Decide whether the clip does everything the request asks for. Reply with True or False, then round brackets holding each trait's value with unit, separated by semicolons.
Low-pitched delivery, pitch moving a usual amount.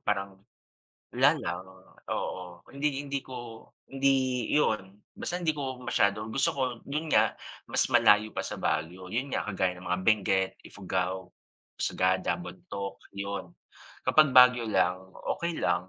False (100 Hz; 6.7 semitones)